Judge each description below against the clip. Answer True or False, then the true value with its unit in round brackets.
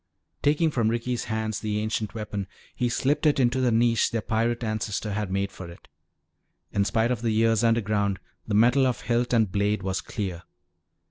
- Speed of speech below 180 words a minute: False (185 wpm)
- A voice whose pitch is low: True (110 Hz)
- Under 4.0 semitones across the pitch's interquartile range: True (2.5 semitones)